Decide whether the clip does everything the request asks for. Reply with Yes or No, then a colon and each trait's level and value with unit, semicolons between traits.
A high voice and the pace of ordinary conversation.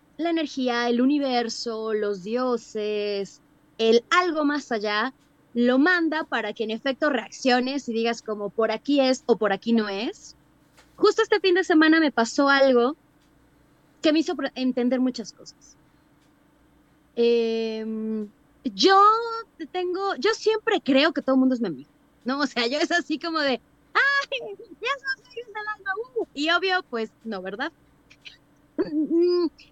Yes: very high, 260 Hz; average, 150 wpm